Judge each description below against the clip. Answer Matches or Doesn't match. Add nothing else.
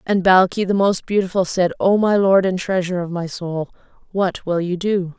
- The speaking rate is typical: Doesn't match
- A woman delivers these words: Matches